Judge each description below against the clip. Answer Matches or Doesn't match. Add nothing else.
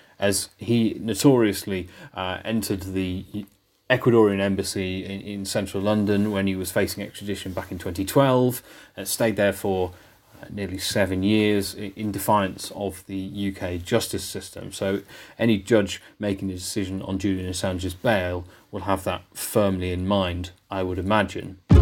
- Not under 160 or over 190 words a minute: Doesn't match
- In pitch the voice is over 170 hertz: Doesn't match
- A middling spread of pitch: Doesn't match